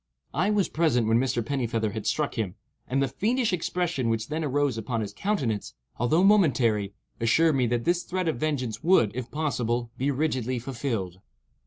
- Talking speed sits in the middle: Yes, average, 175 wpm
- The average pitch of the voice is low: Yes, low, 130 Hz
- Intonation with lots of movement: Yes, wide, 5.7 semitones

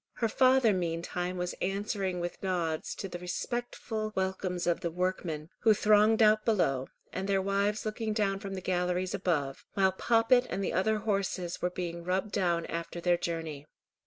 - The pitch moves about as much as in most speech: Yes, average, 3.3 semitones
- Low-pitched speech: No, medium, 185 Hz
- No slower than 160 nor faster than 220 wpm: Yes, average, 170 wpm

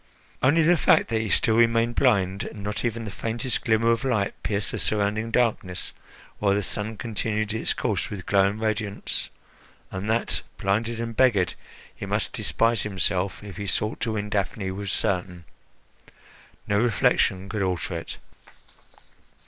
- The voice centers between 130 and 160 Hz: No, low, 105 Hz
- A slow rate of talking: No, average, 155 wpm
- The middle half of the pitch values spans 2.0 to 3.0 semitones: Yes, narrow, 2.6 semitones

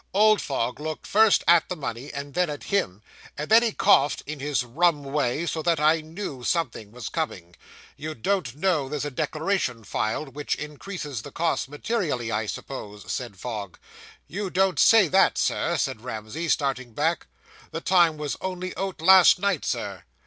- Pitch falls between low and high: Yes, medium, 150 Hz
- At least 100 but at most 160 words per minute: No, average, 175 wpm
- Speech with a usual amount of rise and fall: No, wide, 5.7 semitones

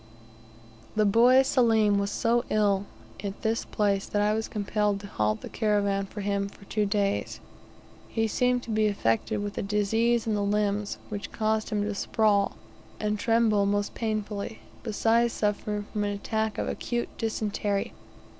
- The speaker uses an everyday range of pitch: No, narrow, 1.6 semitones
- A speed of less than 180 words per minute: Yes, average, 165 wpm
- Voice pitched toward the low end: No, high, 210 Hz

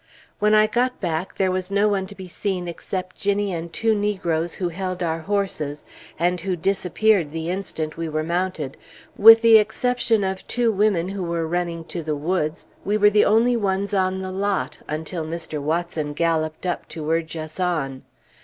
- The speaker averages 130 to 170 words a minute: No, average, 185 wpm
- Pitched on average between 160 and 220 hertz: Yes, medium, 185 Hz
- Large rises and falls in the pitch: No, average, 3.7 semitones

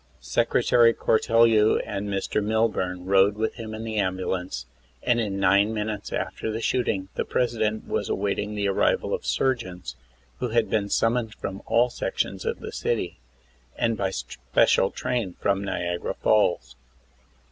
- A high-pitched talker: No, low, 105 Hz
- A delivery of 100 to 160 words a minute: Yes, average, 150 wpm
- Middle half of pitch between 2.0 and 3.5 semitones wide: Yes, average, 2.9 semitones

